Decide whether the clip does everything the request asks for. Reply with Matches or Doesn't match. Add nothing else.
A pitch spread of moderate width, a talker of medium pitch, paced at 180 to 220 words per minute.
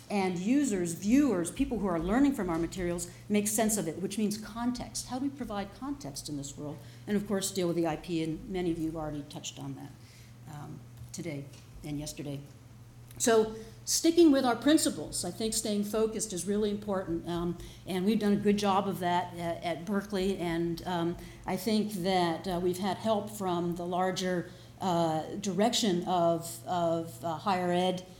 Matches